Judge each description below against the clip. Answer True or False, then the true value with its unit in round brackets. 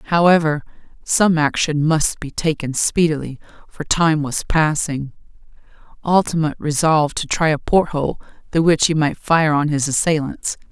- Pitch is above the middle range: False (155 Hz)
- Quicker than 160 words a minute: False (145 wpm)